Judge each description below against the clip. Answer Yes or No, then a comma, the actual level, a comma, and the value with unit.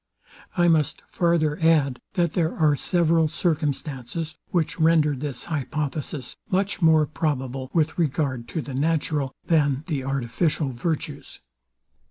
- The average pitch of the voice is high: No, medium, 155 Hz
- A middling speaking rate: No, slow, 125 wpm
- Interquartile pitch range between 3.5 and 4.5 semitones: No, average, 3.1 semitones